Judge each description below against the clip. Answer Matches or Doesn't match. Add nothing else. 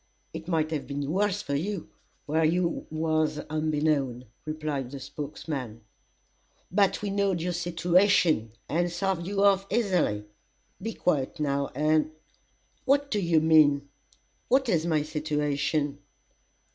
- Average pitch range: Matches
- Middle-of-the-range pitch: Matches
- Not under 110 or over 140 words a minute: Matches